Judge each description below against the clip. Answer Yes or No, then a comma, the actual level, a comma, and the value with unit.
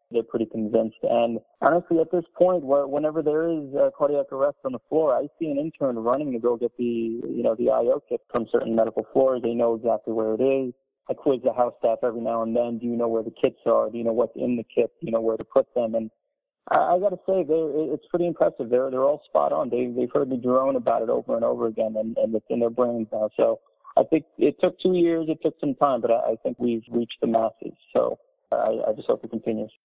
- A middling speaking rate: No, fast, 260 wpm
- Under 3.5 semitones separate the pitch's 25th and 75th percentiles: No, average, 5.3 semitones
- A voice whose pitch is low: Yes, low, 125 Hz